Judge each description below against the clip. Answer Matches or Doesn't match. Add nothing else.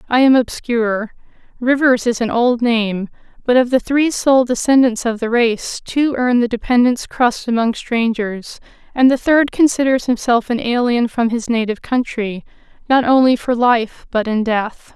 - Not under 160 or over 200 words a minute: Matches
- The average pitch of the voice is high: Matches